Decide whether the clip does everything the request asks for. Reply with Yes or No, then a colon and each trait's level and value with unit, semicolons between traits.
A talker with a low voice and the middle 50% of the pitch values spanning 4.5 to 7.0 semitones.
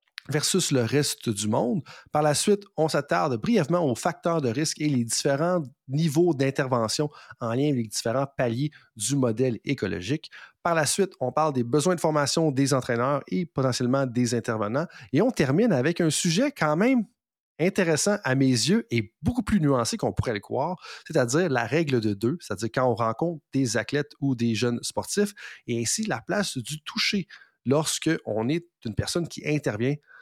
No: medium, 145 Hz; average, 5.2 semitones